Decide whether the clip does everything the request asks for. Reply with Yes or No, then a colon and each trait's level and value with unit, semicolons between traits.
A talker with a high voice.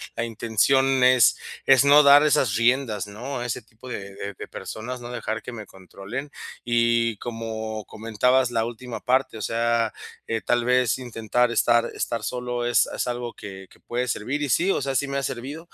No: low, 120 Hz